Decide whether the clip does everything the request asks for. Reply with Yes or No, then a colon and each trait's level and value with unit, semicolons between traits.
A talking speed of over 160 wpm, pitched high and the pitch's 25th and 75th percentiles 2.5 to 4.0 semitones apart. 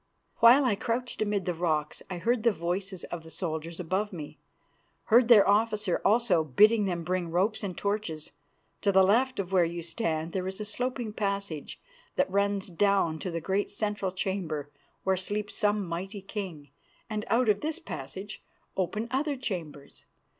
Yes: average, 170 wpm; high, 195 Hz; average, 3.7 semitones